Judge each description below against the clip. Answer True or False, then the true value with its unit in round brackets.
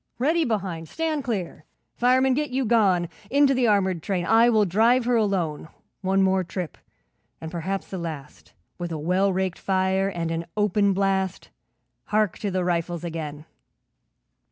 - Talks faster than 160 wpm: False (155 wpm)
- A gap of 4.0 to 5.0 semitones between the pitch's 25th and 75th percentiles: True (4.5 semitones)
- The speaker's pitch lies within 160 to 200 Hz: True (190 Hz)